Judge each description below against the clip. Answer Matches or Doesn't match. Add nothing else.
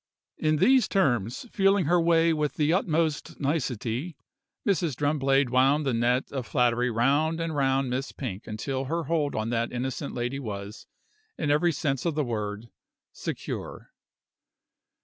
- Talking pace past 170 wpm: Doesn't match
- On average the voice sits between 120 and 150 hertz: Matches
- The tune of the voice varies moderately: Matches